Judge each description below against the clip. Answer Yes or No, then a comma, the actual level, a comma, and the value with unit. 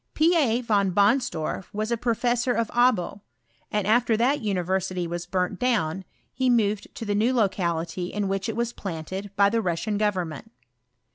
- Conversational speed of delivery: Yes, average, 170 wpm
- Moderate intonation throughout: Yes, average, 4.2 semitones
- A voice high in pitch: Yes, high, 205 Hz